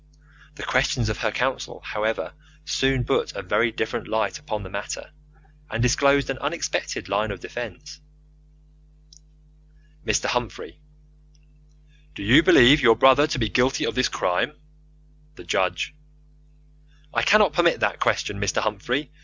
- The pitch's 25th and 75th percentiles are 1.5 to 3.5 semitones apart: No, average, 4.6 semitones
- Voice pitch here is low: Yes, low, 125 Hz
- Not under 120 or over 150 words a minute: Yes, slow, 135 wpm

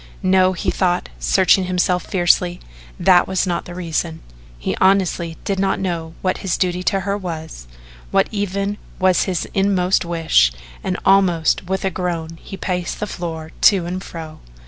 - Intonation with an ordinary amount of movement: No, narrow, 2.0 semitones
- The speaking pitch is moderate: Yes, medium, 180 Hz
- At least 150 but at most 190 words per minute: Yes, average, 165 wpm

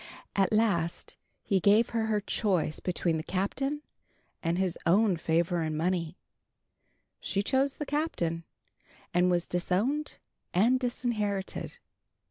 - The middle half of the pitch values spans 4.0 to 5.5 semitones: Yes, average, 4.8 semitones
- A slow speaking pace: Yes, slow, 120 wpm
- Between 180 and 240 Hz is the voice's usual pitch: Yes, high, 190 Hz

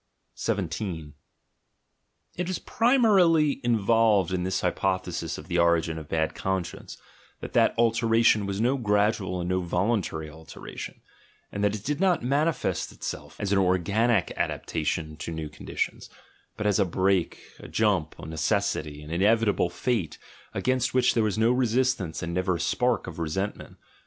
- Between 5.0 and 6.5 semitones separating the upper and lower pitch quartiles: Yes, wide, 5.4 semitones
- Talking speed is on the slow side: No, average, 155 wpm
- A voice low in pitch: Yes, low, 100 Hz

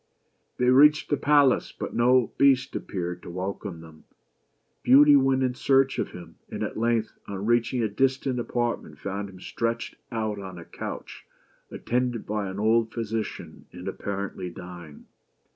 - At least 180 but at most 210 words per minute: No, average, 160 wpm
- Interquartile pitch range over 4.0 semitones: Yes, average, 4.7 semitones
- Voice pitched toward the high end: No, low, 115 Hz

